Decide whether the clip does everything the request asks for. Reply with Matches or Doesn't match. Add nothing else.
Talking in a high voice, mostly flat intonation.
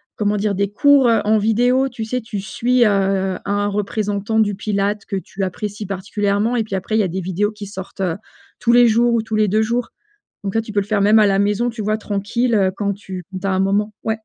Matches